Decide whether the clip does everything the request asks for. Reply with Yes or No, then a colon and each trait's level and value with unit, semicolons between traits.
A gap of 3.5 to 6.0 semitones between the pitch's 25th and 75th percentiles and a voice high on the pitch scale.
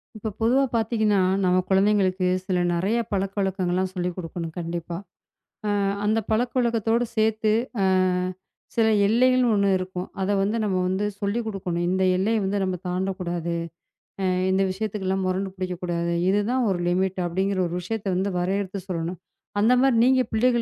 No: average, 3.0 semitones; high, 195 Hz